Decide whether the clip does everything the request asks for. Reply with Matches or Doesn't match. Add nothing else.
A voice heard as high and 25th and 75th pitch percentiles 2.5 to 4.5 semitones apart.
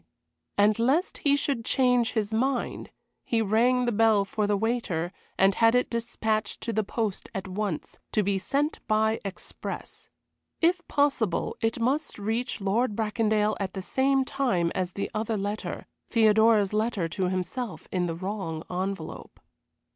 Matches